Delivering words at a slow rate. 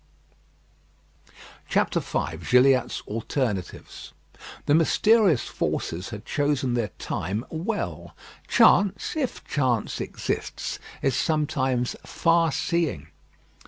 Yes: slow, 85 wpm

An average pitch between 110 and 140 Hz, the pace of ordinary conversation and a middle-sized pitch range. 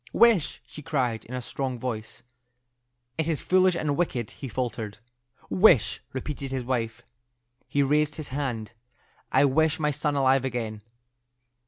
Yes: low, 135 Hz; average, 145 wpm; average, 4.0 semitones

